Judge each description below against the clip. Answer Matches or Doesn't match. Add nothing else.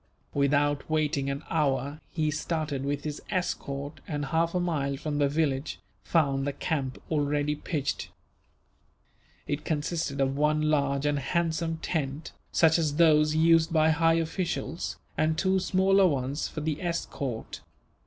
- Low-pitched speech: Doesn't match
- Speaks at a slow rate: Doesn't match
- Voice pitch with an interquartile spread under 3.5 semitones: Matches